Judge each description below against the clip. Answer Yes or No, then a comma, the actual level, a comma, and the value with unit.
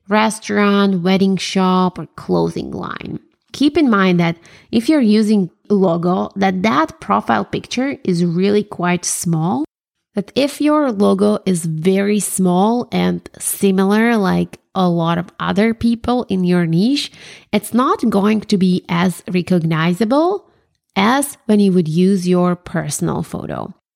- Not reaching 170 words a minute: Yes, average, 140 wpm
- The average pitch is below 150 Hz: No, high, 195 Hz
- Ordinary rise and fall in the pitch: Yes, average, 3.7 semitones